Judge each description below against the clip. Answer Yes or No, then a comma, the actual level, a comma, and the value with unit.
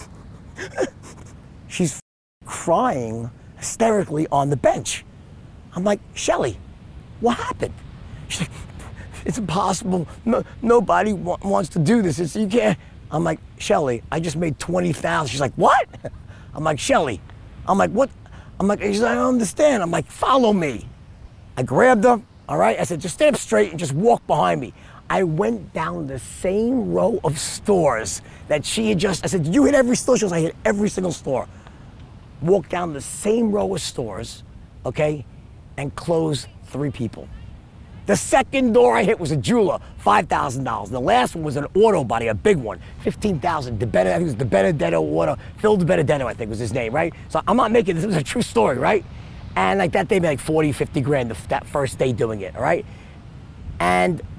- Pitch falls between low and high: Yes, medium, 165 Hz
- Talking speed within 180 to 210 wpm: Yes, average, 190 wpm